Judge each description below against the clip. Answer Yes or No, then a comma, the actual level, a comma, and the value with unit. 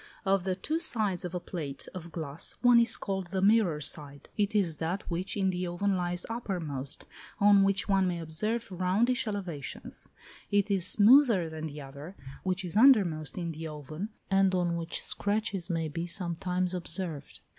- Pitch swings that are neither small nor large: Yes, average, 3.5 semitones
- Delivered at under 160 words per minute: No, average, 175 wpm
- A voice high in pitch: No, medium, 180 Hz